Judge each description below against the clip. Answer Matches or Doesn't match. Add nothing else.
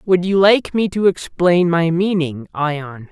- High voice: Doesn't match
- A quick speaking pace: Doesn't match